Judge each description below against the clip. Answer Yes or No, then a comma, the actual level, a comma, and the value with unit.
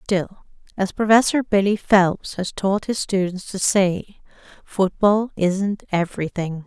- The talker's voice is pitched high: Yes, high, 195 Hz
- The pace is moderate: No, slow, 125 wpm